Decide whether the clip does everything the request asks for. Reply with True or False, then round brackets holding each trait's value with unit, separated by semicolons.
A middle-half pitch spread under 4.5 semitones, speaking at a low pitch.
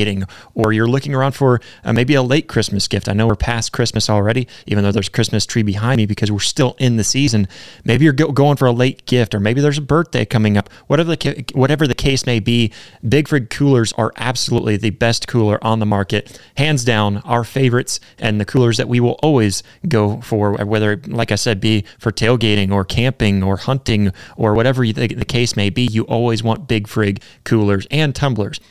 True (3.4 semitones; 115 Hz)